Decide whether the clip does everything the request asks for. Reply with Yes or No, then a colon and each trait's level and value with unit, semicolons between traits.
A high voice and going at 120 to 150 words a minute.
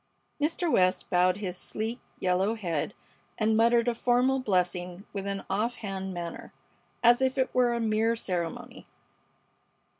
Yes: high, 215 Hz; average, 140 wpm